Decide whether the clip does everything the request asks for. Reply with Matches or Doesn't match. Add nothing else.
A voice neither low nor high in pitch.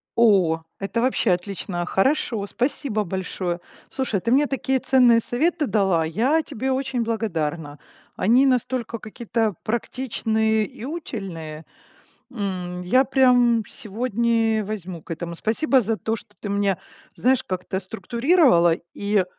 Doesn't match